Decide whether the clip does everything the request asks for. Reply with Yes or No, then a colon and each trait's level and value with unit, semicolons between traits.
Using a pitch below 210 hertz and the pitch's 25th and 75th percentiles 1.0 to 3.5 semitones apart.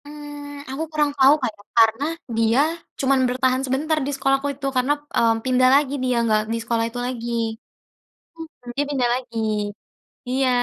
No: very high, 260 Hz; average, 2.9 semitones